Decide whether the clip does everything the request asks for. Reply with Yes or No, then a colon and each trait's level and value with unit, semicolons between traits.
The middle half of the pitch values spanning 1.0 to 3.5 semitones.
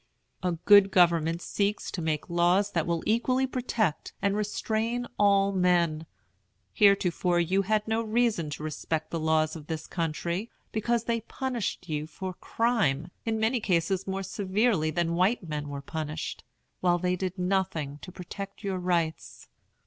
No: average, 4.2 semitones